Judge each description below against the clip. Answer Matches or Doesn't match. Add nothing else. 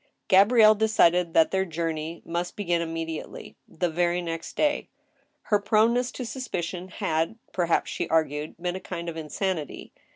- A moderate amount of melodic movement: Matches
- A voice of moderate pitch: Matches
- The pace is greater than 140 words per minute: Matches